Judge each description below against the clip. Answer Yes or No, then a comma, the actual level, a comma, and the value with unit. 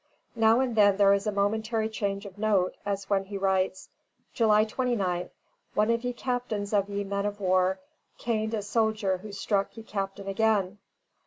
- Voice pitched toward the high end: Yes, high, 205 Hz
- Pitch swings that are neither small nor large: No, narrow, 2.0 semitones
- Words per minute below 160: No, average, 175 wpm